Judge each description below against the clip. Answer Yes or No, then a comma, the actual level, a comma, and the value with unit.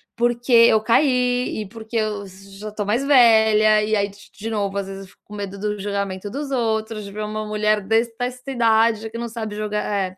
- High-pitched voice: Yes, high, 215 Hz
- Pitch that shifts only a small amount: Yes, narrow, 2.1 semitones